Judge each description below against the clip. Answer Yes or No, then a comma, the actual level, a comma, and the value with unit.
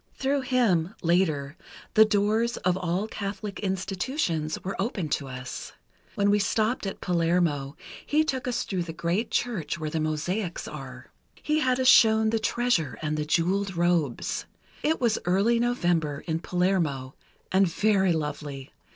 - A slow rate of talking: No, average, 150 wpm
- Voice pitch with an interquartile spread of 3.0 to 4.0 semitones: No, average, 5.3 semitones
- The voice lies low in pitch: No, medium, 185 Hz